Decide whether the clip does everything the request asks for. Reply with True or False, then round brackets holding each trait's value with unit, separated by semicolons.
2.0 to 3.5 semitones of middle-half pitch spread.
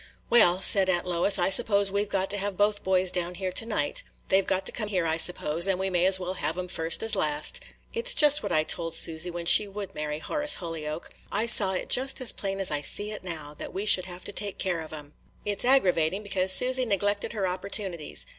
True (3.1 semitones)